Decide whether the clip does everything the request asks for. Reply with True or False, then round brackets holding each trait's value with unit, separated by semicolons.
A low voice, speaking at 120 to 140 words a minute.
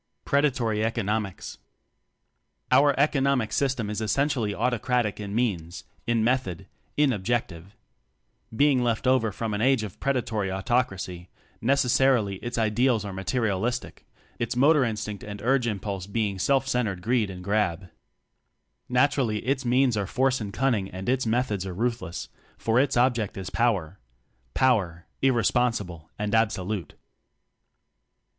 True (115 Hz; 135 wpm)